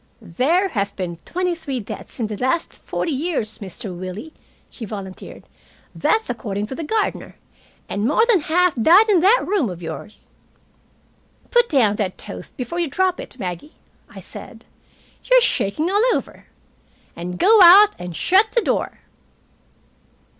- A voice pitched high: Yes, very high, 290 Hz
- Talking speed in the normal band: Yes, average, 160 wpm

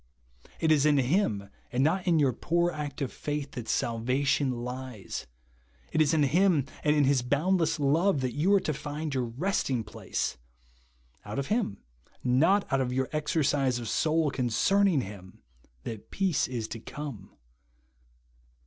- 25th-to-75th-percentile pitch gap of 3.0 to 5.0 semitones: Yes, average, 4.1 semitones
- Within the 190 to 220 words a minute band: No, average, 165 wpm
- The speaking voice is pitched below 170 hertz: Yes, medium, 140 Hz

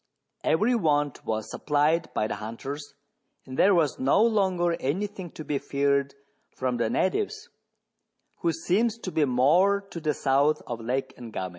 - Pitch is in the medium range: Yes, medium, 150 Hz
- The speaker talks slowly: No, average, 160 wpm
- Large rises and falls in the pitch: Yes, wide, 6.0 semitones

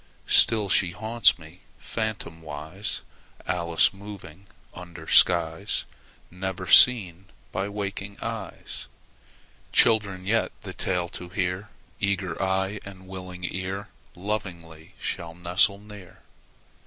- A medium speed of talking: No, slow, 105 wpm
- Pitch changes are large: No, narrow, 2.6 semitones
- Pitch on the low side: Yes, very low, 95 Hz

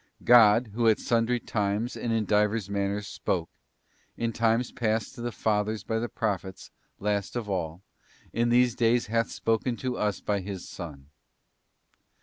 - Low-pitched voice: Yes, low, 110 Hz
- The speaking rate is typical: Yes, average, 160 wpm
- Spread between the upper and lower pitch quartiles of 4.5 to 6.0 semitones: No, narrow, 2.5 semitones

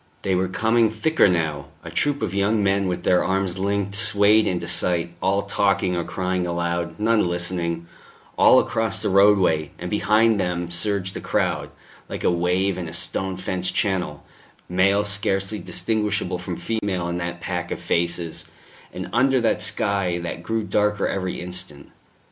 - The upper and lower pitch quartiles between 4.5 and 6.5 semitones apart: No, average, 2.8 semitones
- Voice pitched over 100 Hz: No, very low, 95 Hz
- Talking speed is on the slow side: No, average, 165 wpm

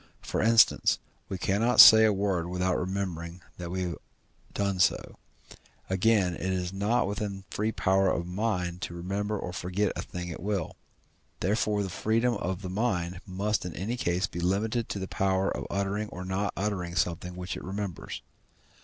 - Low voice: Yes, very low, 95 Hz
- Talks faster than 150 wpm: Yes, average, 180 wpm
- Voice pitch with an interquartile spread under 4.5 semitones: Yes, narrow, 2.5 semitones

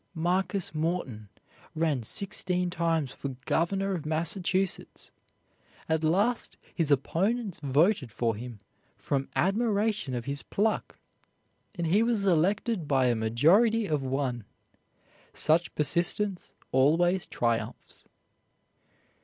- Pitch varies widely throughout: Yes, wide, 6.0 semitones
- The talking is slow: Yes, slow, 105 wpm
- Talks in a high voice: No, medium, 165 Hz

